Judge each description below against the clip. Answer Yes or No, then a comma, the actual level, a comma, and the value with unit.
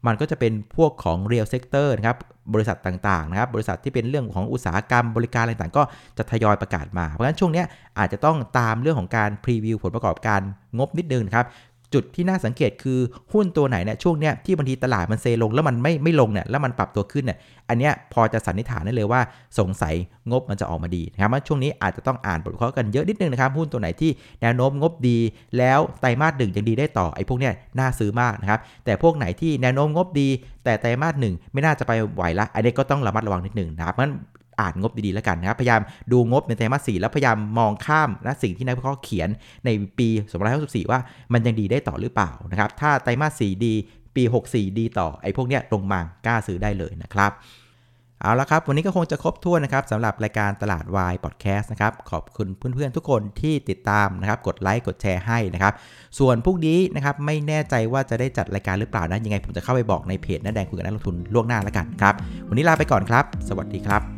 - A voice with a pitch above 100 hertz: Yes, low, 115 Hz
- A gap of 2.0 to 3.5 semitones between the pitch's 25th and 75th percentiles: No, average, 4.6 semitones